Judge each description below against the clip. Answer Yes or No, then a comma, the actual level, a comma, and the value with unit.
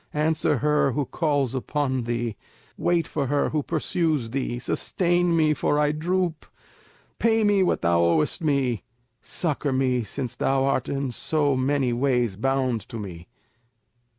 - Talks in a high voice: No, medium, 140 Hz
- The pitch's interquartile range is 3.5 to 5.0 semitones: Yes, average, 4.0 semitones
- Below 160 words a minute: Yes, average, 150 wpm